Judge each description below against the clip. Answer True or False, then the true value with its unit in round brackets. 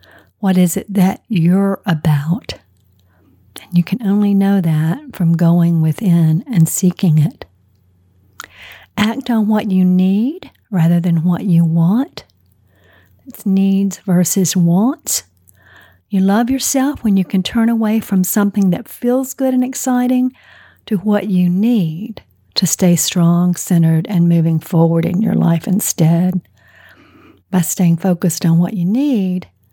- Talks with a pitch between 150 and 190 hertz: True (185 Hz)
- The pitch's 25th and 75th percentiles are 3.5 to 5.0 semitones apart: True (3.8 semitones)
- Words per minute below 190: True (140 wpm)